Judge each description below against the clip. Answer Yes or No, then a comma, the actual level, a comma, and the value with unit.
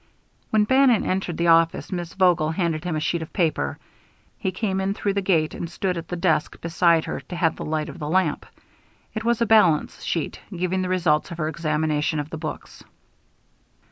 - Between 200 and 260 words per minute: Yes, fast, 205 wpm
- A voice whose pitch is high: No, medium, 170 Hz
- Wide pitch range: No, average, 3.1 semitones